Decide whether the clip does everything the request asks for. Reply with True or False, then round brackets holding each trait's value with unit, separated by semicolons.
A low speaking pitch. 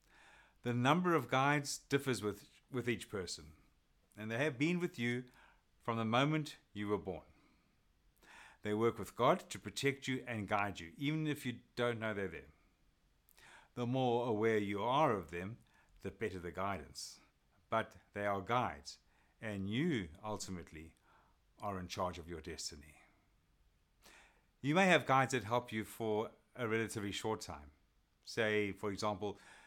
True (105 Hz)